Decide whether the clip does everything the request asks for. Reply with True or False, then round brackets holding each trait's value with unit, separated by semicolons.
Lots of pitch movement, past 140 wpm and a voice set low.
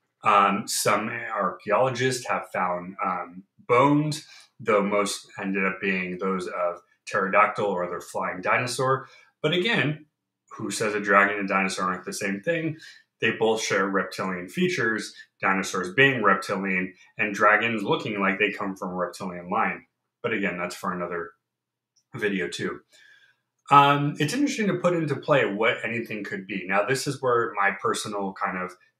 True (6.0 semitones; 155 wpm; 105 Hz)